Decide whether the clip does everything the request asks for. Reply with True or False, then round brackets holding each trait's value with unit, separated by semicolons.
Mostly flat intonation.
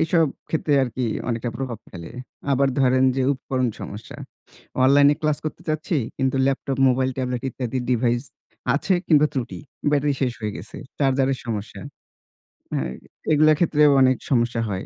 False (3.2 semitones)